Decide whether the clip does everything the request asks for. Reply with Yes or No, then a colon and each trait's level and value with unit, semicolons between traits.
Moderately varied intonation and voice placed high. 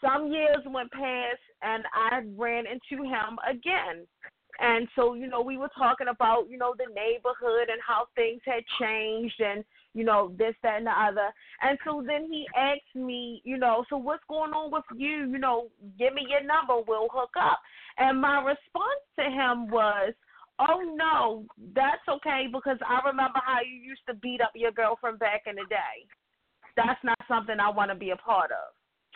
Yes: average, 3.4 semitones; very high, 250 Hz